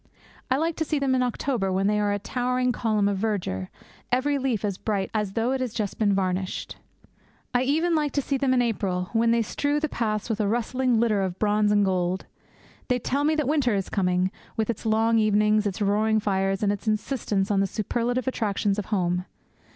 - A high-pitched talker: Yes, high, 215 Hz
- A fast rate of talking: Yes, fast, 215 wpm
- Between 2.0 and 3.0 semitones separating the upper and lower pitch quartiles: No, average, 4.0 semitones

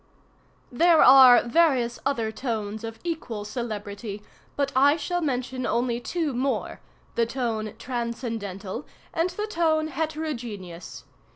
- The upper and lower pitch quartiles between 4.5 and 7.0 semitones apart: Yes, average, 5.2 semitones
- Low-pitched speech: No, high, 245 Hz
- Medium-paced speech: No, slow, 110 wpm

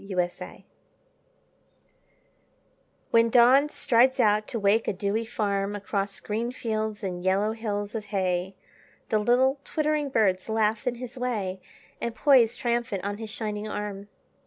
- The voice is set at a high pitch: Yes, high, 215 Hz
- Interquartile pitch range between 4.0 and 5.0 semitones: No, average, 2.9 semitones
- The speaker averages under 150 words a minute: Yes, average, 140 wpm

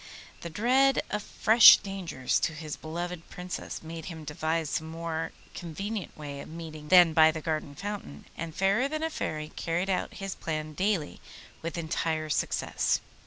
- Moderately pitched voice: Yes, medium, 165 Hz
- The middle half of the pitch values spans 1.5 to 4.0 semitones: Yes, average, 3.6 semitones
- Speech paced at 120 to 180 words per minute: Yes, average, 165 wpm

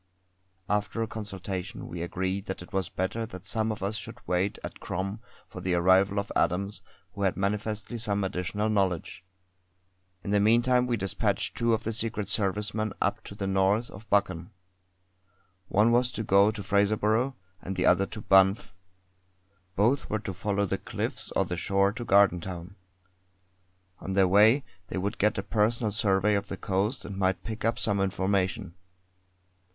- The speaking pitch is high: No, low, 100 Hz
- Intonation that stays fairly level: Yes, narrow, 2.2 semitones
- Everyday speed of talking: Yes, average, 170 wpm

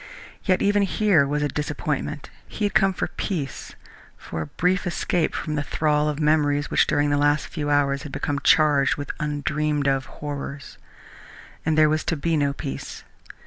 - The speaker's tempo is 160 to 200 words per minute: Yes, average, 180 wpm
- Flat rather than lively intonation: Yes, narrow, 1.6 semitones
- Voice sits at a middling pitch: Yes, medium, 150 Hz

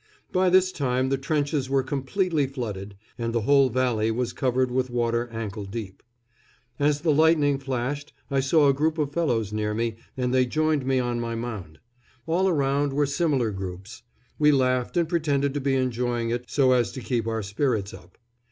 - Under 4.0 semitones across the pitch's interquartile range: Yes, average, 3.6 semitones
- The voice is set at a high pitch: No, low, 130 Hz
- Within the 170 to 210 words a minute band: Yes, average, 185 wpm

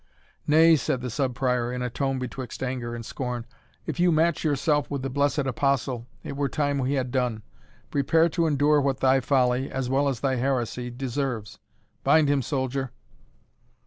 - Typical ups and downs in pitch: No, narrow, 2.3 semitones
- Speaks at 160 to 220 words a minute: Yes, average, 175 wpm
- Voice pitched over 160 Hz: No, low, 135 Hz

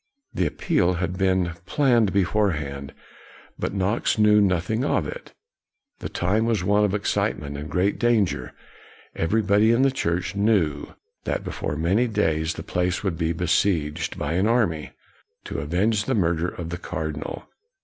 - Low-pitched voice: Yes, very low, 95 Hz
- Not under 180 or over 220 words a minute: No, average, 155 wpm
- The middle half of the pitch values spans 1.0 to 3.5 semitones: No, average, 4.3 semitones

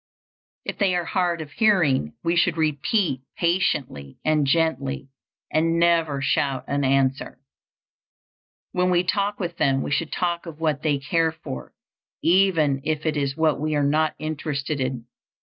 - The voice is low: No, medium, 155 Hz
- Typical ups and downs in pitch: Yes, average, 3.5 semitones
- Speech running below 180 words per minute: Yes, average, 155 wpm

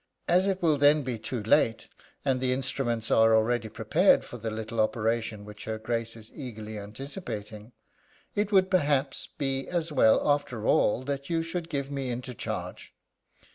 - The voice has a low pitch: Yes, low, 125 Hz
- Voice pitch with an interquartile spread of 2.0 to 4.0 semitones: No, average, 4.4 semitones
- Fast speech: No, average, 170 wpm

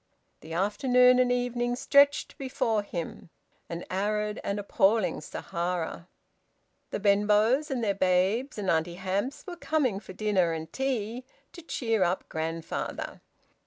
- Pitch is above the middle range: Yes, high, 210 Hz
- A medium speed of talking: No, slow, 130 wpm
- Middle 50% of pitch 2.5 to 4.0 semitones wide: No, average, 5.3 semitones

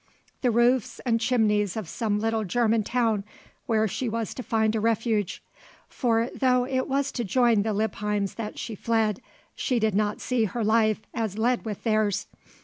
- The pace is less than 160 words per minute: No, average, 175 wpm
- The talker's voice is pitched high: Yes, high, 225 Hz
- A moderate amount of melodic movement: No, narrow, 2.1 semitones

